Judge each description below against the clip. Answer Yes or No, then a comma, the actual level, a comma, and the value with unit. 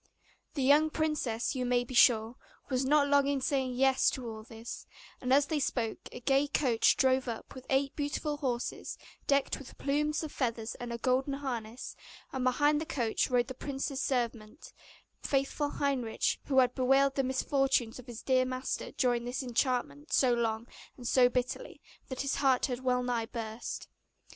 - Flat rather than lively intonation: Yes, narrow, 2.3 semitones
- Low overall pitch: No, very high, 260 Hz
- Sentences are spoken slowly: No, average, 175 wpm